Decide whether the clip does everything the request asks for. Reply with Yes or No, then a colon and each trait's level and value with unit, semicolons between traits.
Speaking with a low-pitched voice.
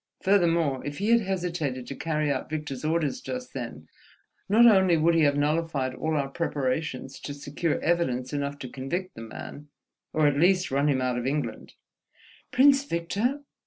No: medium, 155 Hz